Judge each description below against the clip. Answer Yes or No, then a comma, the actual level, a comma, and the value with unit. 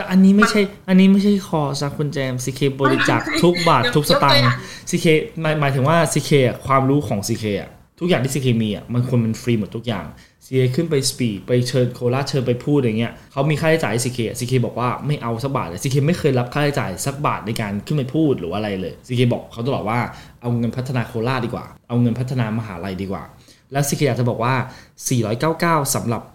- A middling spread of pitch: Yes, average, 4.0 semitones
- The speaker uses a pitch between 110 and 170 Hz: Yes, low, 130 Hz